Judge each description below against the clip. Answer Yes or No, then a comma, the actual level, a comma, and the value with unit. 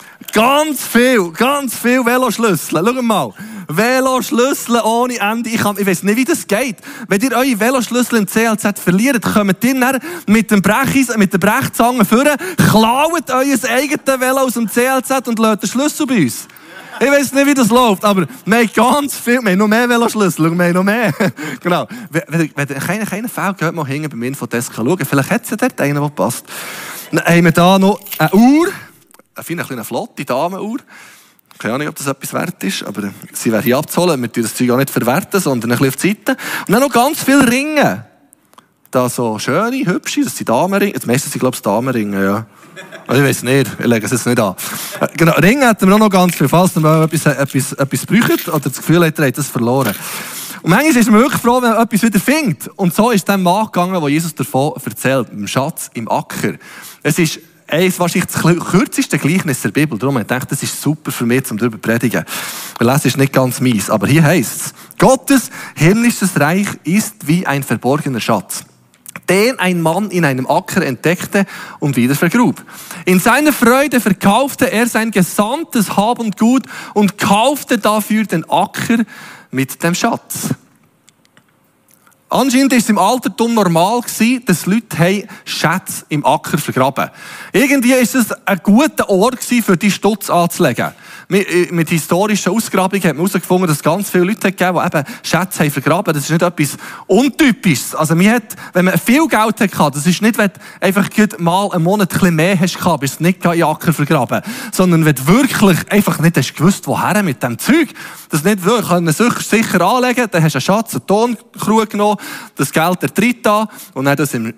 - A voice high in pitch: Yes, high, 195 Hz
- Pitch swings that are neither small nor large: No, wide, 6.9 semitones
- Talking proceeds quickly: Yes, fast, 195 wpm